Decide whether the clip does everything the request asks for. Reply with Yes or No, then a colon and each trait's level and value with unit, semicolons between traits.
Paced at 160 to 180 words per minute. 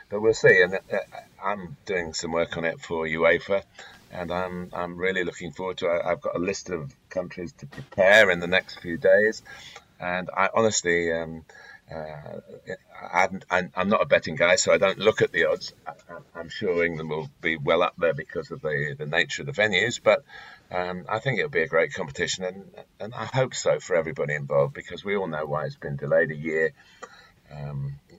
No: average, 200 wpm